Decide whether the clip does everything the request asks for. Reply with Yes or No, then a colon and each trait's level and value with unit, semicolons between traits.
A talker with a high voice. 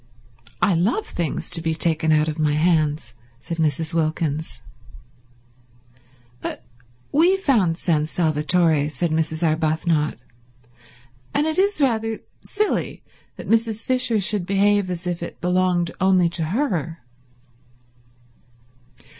No: medium, 170 Hz